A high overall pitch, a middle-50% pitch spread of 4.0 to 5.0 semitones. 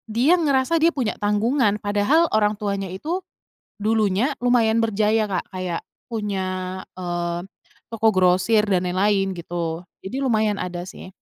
No: high, 205 Hz; average, 3.4 semitones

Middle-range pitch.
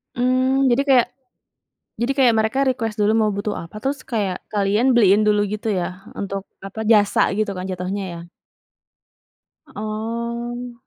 No: high, 215 Hz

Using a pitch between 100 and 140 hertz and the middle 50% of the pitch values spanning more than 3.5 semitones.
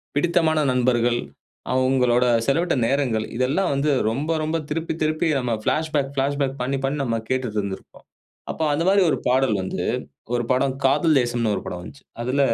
Yes: low, 135 Hz; average, 3.9 semitones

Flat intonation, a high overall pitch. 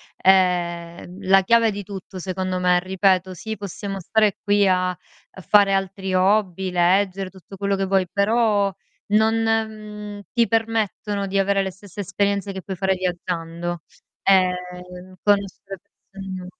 Yes: narrow, 1.8 semitones; high, 195 Hz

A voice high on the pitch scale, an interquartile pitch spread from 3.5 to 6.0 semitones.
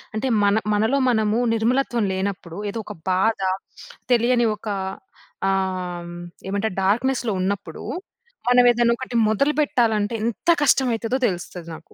Yes: high, 220 Hz; average, 3.8 semitones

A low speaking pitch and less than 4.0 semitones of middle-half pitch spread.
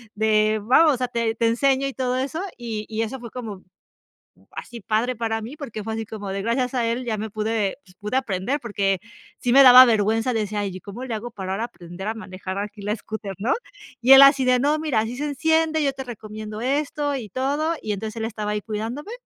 No: high, 230 Hz; average, 3.5 semitones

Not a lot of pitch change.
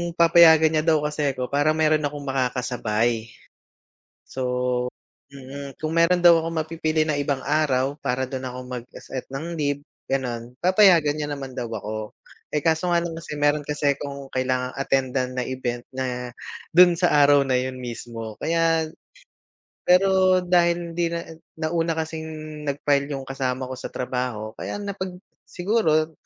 No: average, 4.2 semitones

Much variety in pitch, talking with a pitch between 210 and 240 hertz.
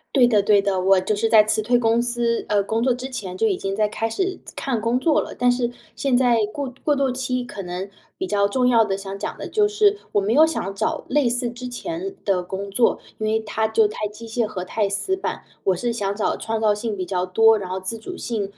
No: average, 3.7 semitones; high, 225 Hz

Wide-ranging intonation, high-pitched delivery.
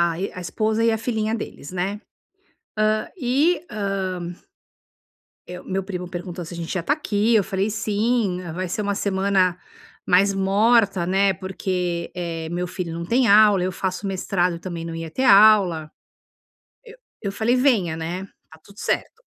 No: average, 3.2 semitones; high, 195 Hz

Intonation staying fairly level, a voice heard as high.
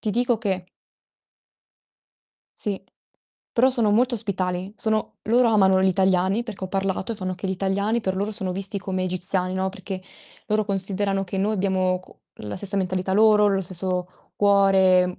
Yes: narrow, 1.9 semitones; high, 195 Hz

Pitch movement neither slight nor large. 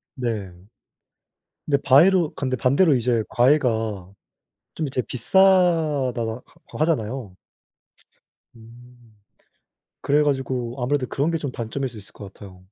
Yes: average, 4.0 semitones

